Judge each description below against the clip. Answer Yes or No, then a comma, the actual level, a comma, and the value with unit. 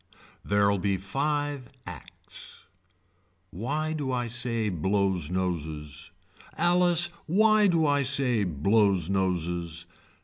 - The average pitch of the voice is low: Yes, low, 105 Hz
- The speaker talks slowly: Yes, slow, 100 wpm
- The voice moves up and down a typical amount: No, wide, 8.3 semitones